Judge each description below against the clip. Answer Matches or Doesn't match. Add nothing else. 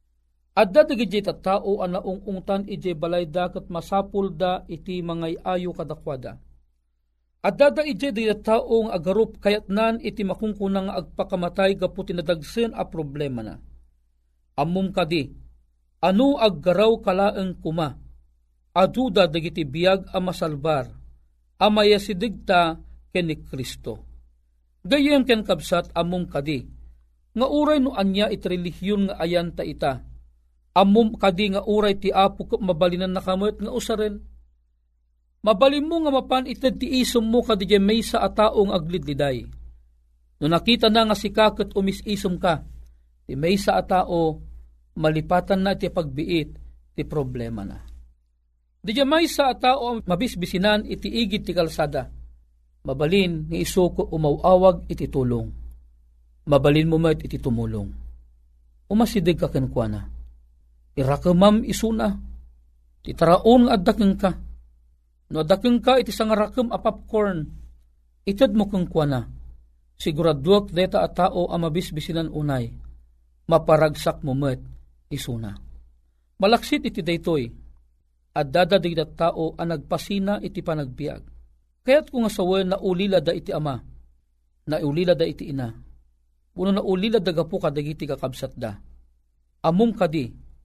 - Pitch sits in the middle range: Matches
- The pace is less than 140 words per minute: Matches